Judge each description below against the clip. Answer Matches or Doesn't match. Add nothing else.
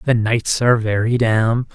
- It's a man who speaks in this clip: Matches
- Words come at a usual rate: Matches